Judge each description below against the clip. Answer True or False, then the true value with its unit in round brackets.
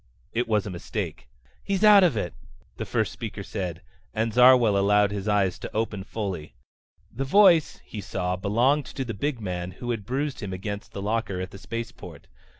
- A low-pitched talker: True (105 Hz)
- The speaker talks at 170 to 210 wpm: True (185 wpm)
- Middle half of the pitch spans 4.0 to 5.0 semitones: True (4.3 semitones)